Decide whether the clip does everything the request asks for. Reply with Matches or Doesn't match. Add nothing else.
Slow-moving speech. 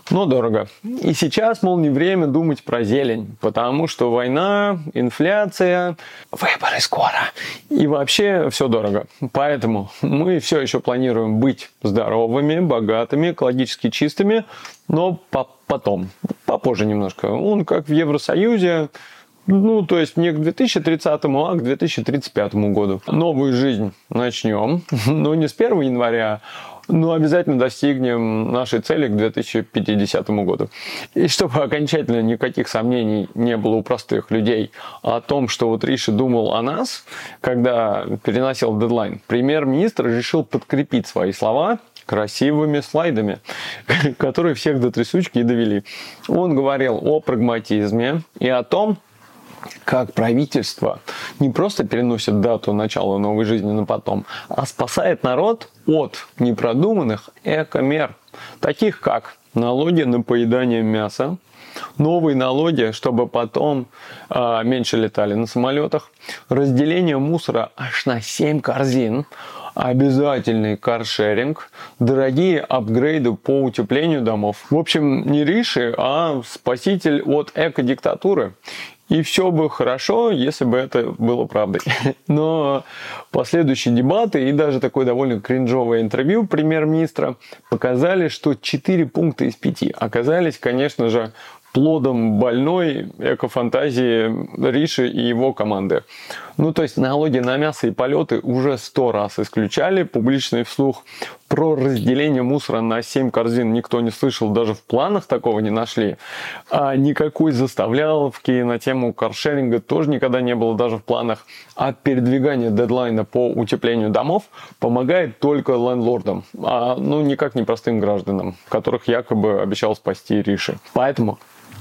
Doesn't match